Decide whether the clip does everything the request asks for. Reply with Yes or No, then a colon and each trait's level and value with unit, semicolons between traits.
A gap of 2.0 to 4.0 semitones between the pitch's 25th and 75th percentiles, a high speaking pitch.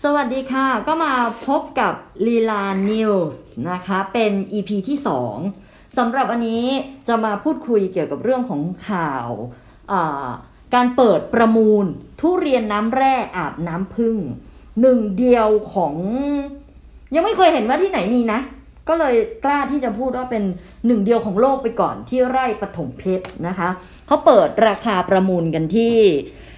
No: wide, 5.4 semitones; high, 230 Hz